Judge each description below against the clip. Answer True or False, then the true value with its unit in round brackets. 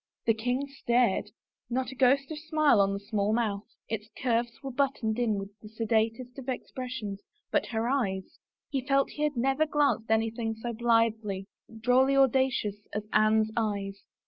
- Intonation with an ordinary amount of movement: True (3.5 semitones)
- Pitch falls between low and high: False (235 Hz)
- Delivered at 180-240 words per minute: False (170 wpm)